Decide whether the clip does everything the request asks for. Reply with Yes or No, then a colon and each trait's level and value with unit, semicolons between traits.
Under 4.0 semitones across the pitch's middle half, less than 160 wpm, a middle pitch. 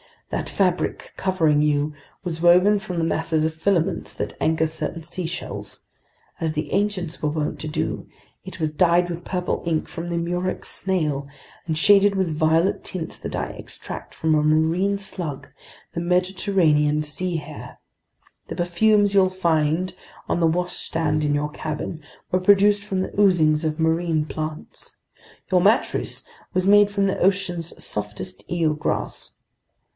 Yes: average, 3.1 semitones; average, 150 wpm; medium, 170 Hz